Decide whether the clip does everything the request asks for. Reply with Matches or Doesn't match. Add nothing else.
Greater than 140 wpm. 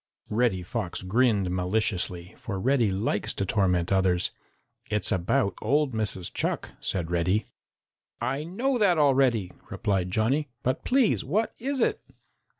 Doesn't match